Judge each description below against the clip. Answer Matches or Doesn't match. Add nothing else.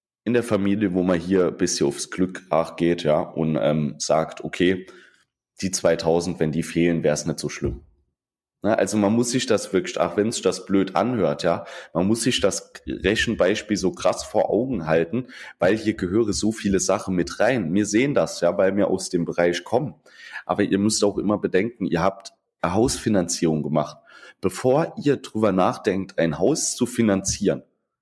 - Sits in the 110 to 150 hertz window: Doesn't match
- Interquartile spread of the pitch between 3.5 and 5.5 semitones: Matches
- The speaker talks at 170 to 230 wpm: Matches